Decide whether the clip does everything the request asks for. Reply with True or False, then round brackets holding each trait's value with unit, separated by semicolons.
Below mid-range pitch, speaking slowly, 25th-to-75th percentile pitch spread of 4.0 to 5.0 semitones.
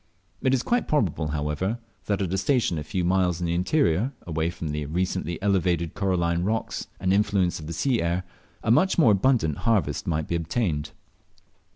False (90 Hz; 190 wpm; 4.3 semitones)